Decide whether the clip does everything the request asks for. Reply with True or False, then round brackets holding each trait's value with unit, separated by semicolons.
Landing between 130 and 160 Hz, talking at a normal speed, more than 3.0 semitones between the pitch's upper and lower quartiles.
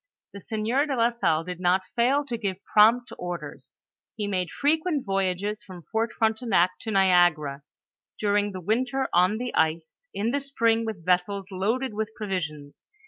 False (205 Hz; 160 wpm; 4.5 semitones)